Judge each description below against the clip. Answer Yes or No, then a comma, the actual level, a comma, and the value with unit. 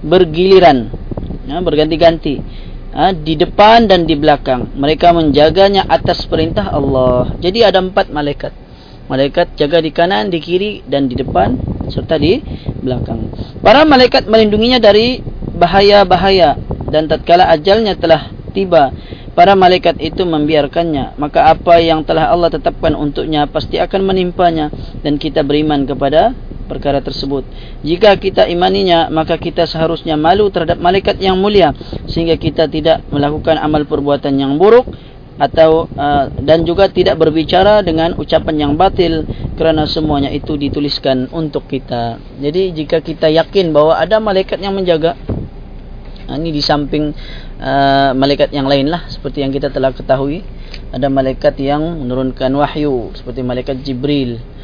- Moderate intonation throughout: Yes, average, 3.8 semitones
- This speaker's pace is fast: No, average, 135 wpm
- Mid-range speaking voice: Yes, medium, 160 Hz